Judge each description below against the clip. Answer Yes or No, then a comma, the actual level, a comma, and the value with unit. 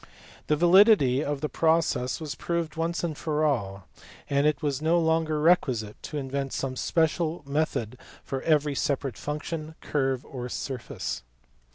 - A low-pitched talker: No, medium, 150 Hz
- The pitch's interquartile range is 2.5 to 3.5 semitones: Yes, average, 3.2 semitones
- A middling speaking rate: Yes, average, 145 wpm